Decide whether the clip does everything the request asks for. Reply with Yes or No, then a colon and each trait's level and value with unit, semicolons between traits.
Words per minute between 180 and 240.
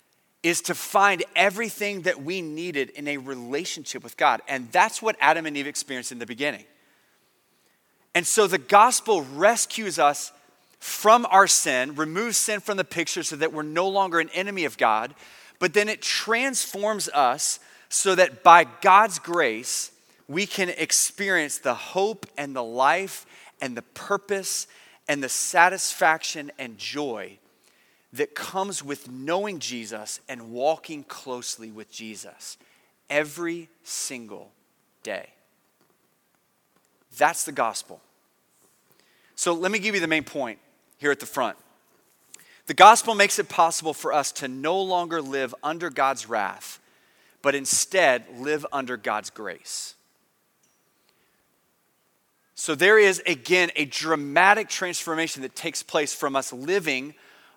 No: average, 140 wpm